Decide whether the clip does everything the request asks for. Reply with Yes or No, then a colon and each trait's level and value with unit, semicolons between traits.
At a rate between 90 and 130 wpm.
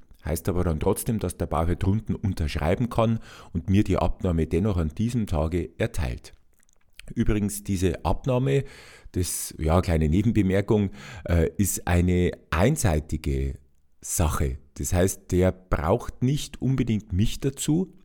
Yes: slow, 125 wpm